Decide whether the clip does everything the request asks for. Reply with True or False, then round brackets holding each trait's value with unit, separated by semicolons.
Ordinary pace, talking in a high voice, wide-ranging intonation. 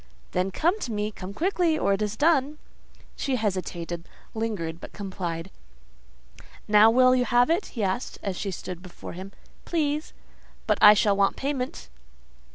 True (160 wpm; 210 Hz; 6.0 semitones)